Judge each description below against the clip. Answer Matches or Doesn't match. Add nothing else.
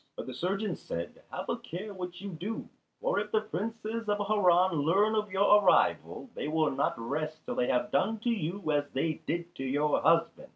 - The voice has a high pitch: Doesn't match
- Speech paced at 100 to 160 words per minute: Doesn't match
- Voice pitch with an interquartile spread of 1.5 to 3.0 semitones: Doesn't match